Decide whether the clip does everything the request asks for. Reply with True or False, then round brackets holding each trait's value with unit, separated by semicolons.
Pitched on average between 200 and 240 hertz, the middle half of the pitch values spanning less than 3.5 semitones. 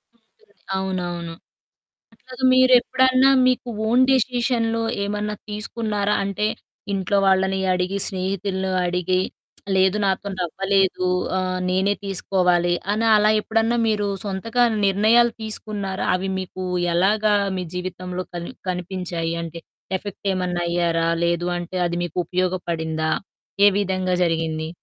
False (190 Hz; 2.9 semitones)